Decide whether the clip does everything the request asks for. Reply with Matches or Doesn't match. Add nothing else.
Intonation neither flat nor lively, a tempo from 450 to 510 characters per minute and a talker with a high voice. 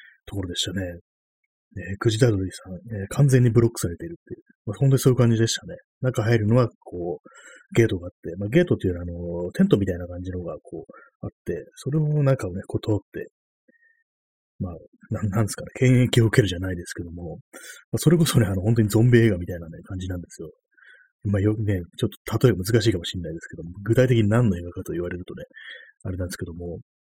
Doesn't match